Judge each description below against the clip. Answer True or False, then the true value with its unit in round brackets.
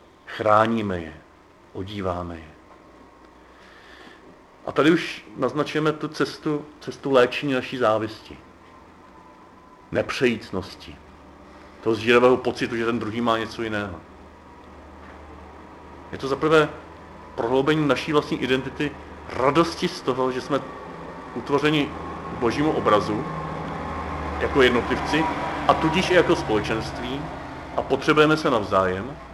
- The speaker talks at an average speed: False (100 wpm)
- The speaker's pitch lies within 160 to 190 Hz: False (115 Hz)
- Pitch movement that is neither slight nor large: False (7.5 semitones)